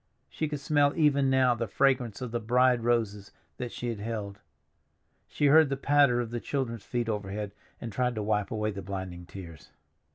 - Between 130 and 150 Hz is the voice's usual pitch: No, low, 120 Hz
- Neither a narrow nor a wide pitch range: Yes, average, 4.2 semitones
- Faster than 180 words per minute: Yes, average, 190 wpm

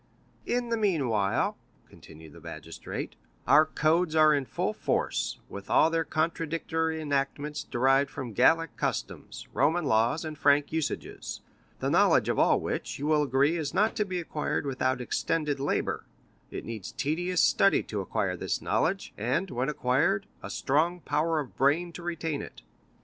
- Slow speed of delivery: No, average, 160 wpm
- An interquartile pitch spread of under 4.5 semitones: Yes, average, 3.6 semitones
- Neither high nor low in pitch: Yes, medium, 150 Hz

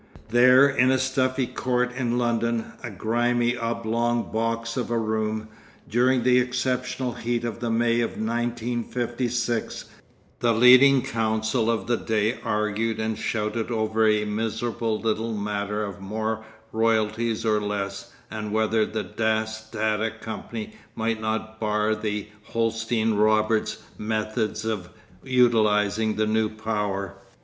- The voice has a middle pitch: No, low, 110 Hz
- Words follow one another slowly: Yes, slow, 130 wpm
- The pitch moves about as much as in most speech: No, narrow, 1.7 semitones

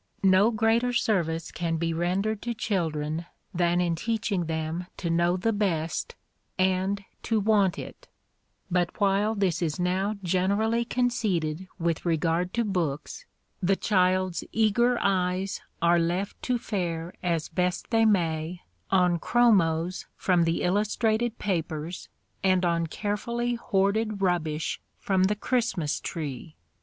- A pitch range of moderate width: Yes, average, 3.9 semitones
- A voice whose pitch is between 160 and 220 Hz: Yes, medium, 185 Hz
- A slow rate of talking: Yes, slow, 130 wpm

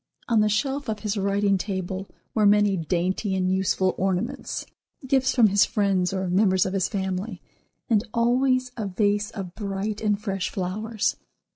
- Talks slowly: No, average, 160 wpm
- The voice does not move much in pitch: Yes, narrow, 2.3 semitones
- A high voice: Yes, high, 200 Hz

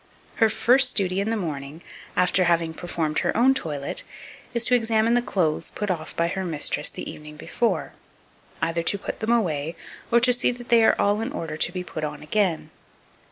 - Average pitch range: No, wide, 5.9 semitones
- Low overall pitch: No, medium, 185 Hz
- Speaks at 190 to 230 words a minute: Yes, average, 195 wpm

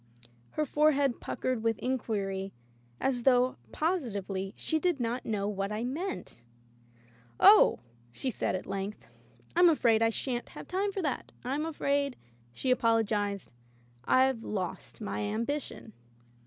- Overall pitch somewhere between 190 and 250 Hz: Yes, high, 240 Hz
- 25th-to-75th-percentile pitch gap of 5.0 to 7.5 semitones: Yes, wide, 5.5 semitones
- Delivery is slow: Yes, slow, 130 wpm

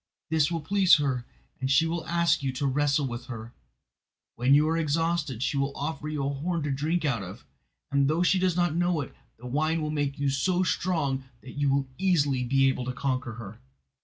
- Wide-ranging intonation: No, average, 3.5 semitones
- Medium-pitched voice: Yes, medium, 145 Hz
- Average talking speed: No, fast, 215 wpm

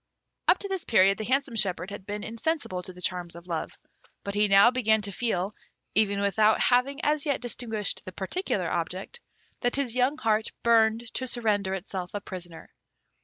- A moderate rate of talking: Yes, average, 180 wpm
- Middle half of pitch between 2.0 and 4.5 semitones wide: Yes, average, 4.2 semitones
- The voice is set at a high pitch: Yes, high, 215 Hz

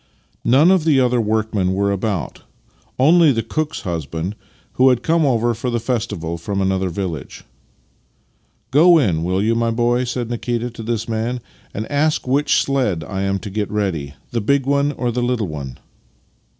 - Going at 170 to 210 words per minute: Yes, average, 190 wpm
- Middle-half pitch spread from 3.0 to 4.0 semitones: No, average, 4.7 semitones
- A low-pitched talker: Yes, low, 115 Hz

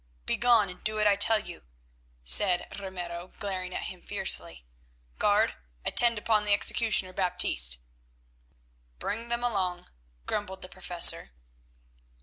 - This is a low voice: No, high, 190 Hz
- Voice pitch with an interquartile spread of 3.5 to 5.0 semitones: No, average, 3.0 semitones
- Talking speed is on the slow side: Yes, slow, 125 wpm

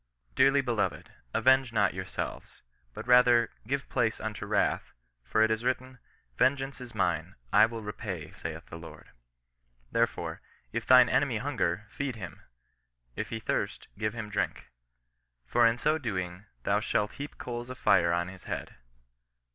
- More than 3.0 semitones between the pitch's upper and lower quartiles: Yes, average, 4.7 semitones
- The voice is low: Yes, low, 110 Hz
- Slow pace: No, average, 160 wpm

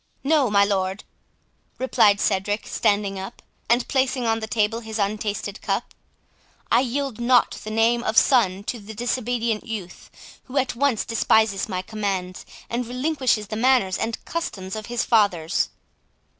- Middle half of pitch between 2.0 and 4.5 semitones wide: Yes, average, 3.4 semitones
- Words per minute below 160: Yes, average, 150 wpm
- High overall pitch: Yes, high, 220 Hz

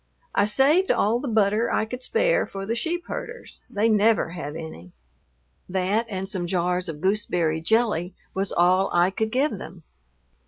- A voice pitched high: Yes, high, 200 Hz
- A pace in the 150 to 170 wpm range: Yes, average, 165 wpm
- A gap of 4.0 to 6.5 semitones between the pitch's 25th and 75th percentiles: Yes, average, 4.4 semitones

